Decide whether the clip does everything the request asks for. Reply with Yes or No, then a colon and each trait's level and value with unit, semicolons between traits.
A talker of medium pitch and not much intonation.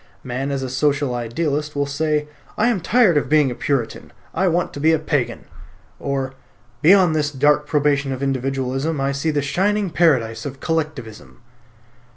No: medium, 145 Hz; average, 3.0 semitones